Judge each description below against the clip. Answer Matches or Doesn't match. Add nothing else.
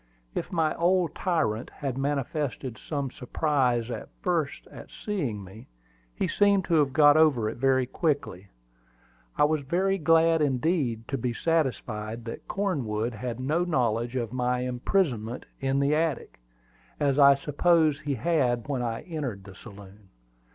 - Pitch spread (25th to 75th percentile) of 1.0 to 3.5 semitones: Doesn't match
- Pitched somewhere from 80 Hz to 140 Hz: Matches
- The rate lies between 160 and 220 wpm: Doesn't match